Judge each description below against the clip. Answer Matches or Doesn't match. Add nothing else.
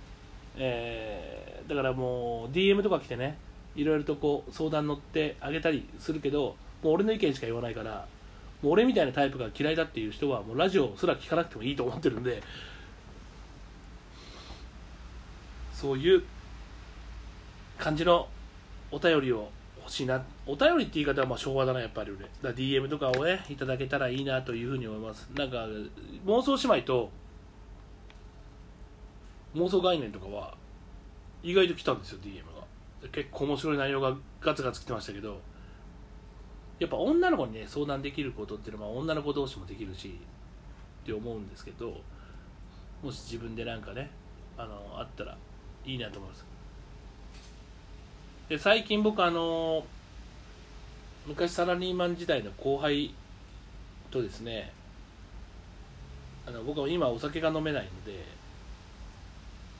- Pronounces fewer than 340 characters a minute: Matches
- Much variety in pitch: Matches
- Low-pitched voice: Matches